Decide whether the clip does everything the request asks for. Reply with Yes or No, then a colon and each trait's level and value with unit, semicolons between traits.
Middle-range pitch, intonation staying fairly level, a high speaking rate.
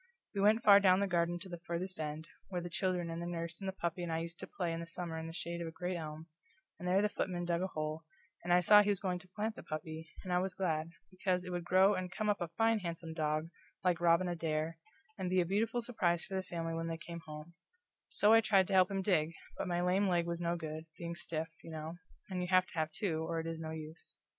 Yes: medium, 175 Hz; narrow, 2.3 semitones; fast, 270 wpm